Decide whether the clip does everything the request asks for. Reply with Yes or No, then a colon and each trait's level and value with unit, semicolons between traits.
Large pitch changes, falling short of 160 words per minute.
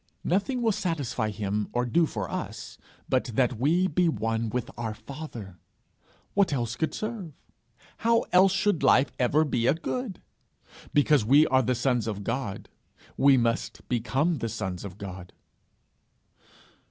Yes: wide, 6.6 semitones; average, 150 wpm